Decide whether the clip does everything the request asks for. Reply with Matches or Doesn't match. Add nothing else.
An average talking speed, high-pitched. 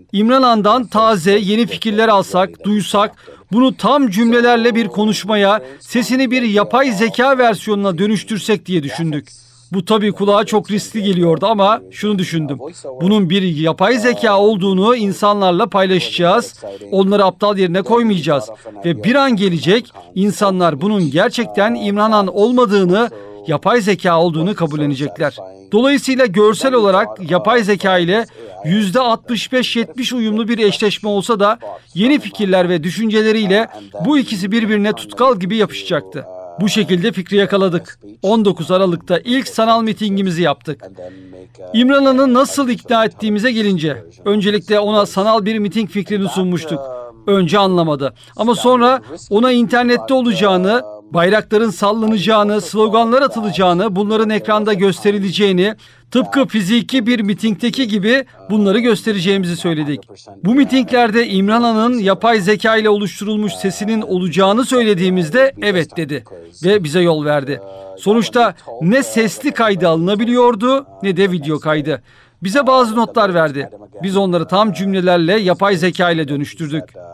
Matches